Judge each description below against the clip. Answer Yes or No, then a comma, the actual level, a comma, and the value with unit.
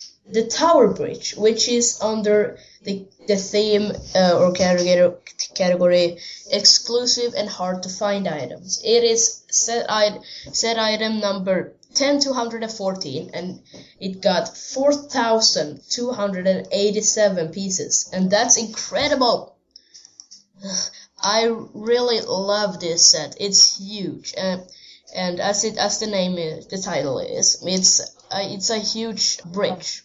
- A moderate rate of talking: No, slow, 120 wpm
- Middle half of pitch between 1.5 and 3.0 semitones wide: No, average, 3.4 semitones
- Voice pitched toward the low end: No, high, 205 Hz